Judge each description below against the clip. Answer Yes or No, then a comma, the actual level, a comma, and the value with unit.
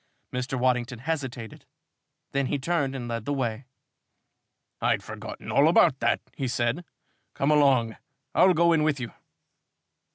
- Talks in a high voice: No, low, 130 Hz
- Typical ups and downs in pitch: Yes, average, 3.4 semitones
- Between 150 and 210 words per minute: No, average, 140 wpm